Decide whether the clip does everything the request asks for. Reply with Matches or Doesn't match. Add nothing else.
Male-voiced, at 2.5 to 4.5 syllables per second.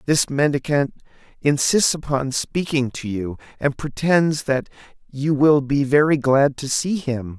Matches